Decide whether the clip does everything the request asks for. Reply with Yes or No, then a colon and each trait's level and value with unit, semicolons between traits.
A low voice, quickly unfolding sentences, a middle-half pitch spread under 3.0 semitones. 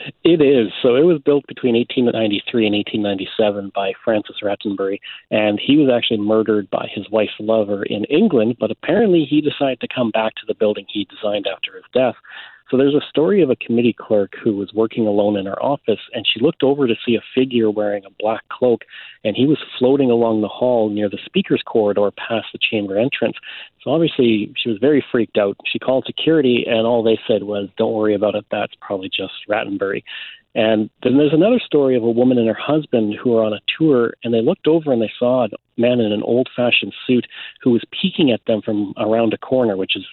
No: low, 115 Hz; fast, 215 wpm; average, 3.3 semitones